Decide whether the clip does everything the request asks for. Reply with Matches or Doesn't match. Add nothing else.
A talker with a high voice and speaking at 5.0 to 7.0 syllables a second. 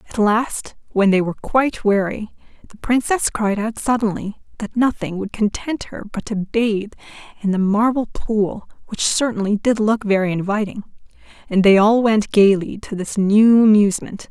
Doesn't match